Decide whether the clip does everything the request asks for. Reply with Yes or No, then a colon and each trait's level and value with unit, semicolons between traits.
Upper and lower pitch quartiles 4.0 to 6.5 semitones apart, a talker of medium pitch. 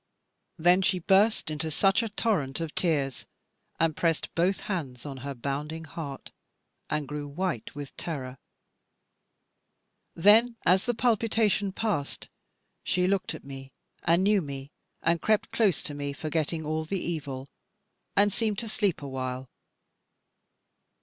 Yes: wide, 5.6 semitones; medium, 165 Hz